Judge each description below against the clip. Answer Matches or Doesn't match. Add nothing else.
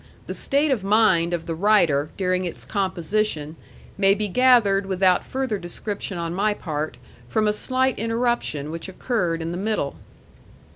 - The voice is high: Matches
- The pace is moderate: Matches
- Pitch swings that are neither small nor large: Matches